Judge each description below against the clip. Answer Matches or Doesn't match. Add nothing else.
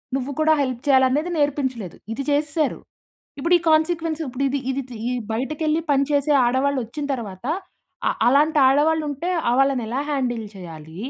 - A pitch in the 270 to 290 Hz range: Matches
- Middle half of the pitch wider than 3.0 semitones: Matches